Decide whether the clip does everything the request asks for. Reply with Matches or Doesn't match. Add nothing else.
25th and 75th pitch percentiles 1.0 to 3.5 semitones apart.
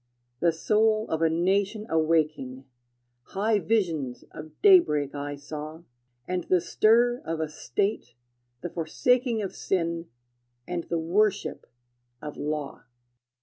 Doesn't match